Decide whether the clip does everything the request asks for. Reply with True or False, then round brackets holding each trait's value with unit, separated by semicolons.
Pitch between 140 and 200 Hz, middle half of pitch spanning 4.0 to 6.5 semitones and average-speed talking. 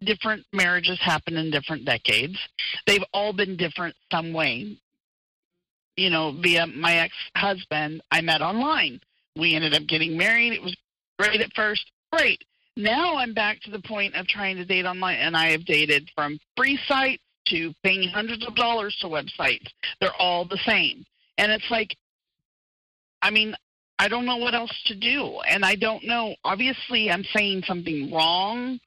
True (190 Hz; 4.9 semitones; 170 wpm)